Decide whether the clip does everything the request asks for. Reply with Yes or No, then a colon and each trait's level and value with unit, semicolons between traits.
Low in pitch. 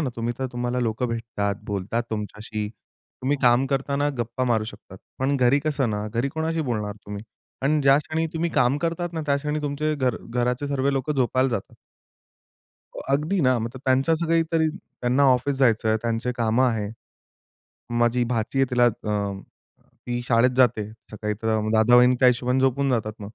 Yes: low, 125 Hz